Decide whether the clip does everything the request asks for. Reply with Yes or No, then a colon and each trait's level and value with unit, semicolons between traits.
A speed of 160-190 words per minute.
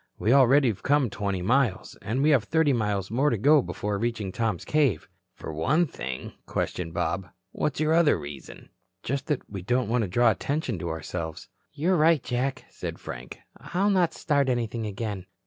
Yes: average, 180 wpm